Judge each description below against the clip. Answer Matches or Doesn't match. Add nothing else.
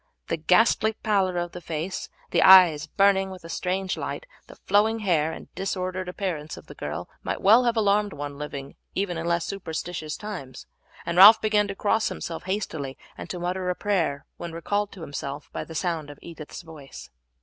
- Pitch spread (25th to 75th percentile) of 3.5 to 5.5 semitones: Matches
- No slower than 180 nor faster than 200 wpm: Matches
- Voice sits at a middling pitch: Matches